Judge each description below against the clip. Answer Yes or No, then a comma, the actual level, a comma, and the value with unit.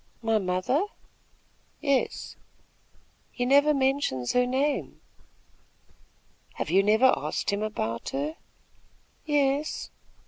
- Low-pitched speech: No, very high, 250 Hz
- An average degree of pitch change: No, wide, 6.4 semitones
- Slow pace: Yes, slow, 95 wpm